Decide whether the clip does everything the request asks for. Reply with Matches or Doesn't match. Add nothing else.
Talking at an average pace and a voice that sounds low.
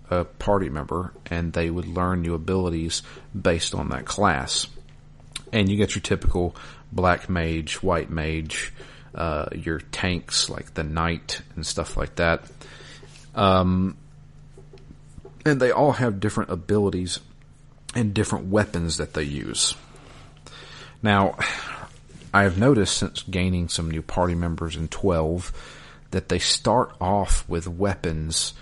Doesn't match